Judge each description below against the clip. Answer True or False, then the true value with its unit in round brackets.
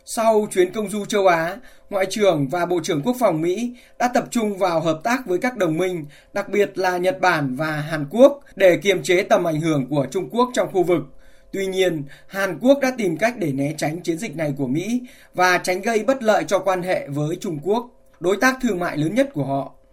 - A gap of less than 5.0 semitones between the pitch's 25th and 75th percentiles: False (5.5 semitones)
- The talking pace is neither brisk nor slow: True (235 wpm)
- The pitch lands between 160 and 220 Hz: True (185 Hz)